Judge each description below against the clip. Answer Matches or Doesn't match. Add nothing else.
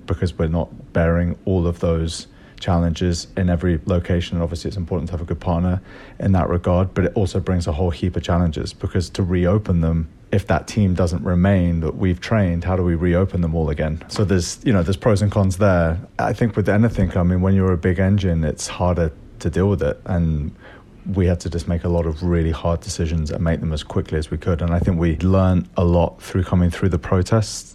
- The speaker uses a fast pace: Matches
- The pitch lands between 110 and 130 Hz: Doesn't match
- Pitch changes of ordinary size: Doesn't match